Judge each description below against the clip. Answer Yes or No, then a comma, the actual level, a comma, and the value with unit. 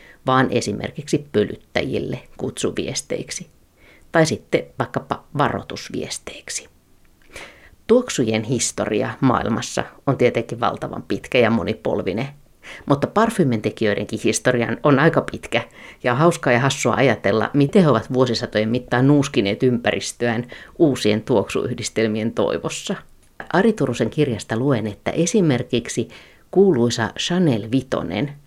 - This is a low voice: Yes, low, 125 Hz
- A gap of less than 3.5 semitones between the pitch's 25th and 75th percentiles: No, average, 4.3 semitones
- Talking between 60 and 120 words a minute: Yes, average, 100 wpm